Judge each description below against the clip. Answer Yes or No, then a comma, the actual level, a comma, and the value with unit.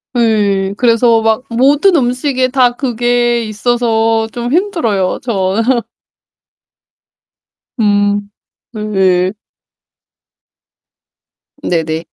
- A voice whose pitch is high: Yes, high, 225 Hz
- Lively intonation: No, average, 3.2 semitones